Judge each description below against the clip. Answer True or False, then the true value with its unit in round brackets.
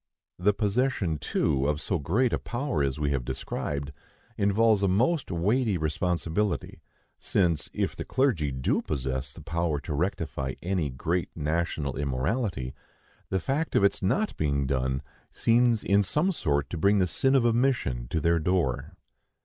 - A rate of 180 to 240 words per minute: False (160 wpm)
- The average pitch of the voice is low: True (85 Hz)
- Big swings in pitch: True (6.8 semitones)